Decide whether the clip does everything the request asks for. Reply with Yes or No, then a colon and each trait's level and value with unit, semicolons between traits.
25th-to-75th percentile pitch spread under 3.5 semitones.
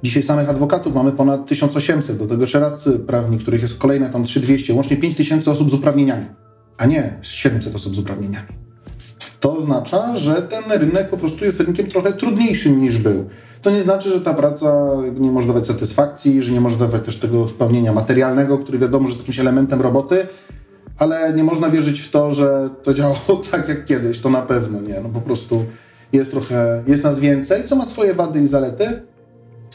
No: average, 4.2 semitones